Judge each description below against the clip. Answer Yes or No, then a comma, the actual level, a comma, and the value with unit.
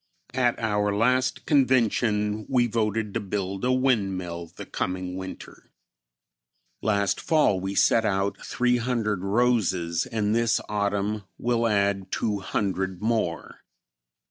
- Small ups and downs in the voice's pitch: No, average, 3.3 semitones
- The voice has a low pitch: Yes, low, 105 Hz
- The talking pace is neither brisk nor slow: No, slow, 115 wpm